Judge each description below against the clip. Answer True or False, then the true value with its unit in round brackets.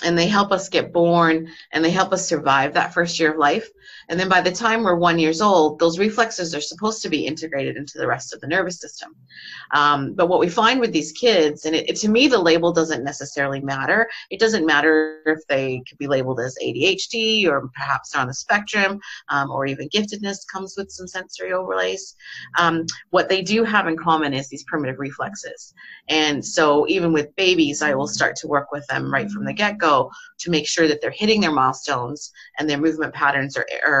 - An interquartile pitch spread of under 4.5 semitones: False (5.0 semitones)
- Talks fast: True (215 wpm)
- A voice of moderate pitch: True (165 Hz)